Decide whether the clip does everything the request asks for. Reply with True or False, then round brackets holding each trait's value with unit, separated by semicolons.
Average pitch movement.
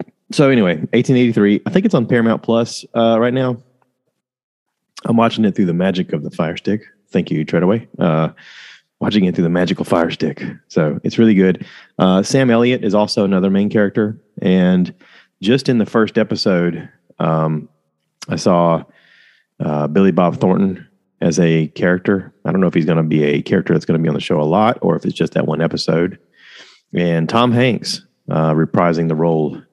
False (5.7 semitones)